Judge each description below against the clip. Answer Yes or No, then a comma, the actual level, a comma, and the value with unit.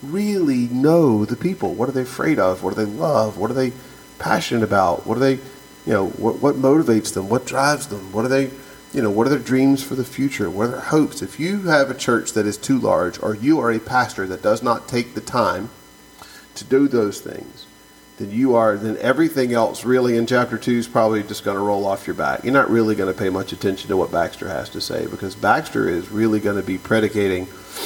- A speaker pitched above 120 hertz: No, low, 115 Hz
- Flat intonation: No, average, 4.3 semitones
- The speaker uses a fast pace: Yes, fast, 240 wpm